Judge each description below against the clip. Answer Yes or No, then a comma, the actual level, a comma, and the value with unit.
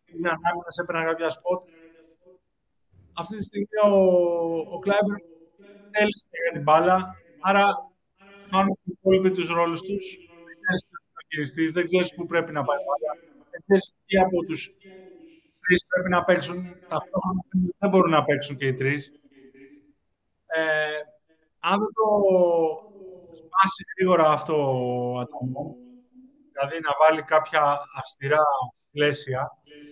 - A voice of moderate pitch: Yes, medium, 170 Hz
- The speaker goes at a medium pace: Yes, average, 130 wpm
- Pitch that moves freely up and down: No, average, 3.8 semitones